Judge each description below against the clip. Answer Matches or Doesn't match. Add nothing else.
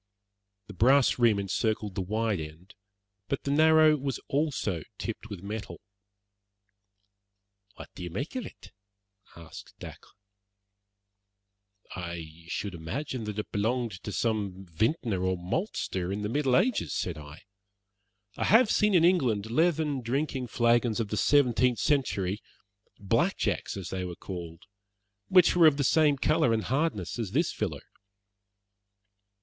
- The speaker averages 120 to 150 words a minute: Matches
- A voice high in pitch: Doesn't match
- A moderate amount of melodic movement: Doesn't match